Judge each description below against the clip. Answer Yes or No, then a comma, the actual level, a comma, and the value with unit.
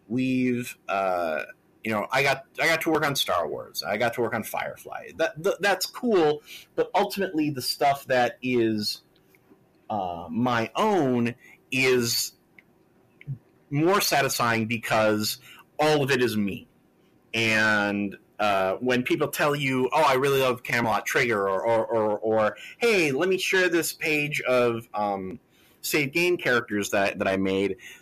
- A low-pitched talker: Yes, low, 125 Hz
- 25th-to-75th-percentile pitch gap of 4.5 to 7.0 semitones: Yes, average, 5.2 semitones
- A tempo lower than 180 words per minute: Yes, average, 155 wpm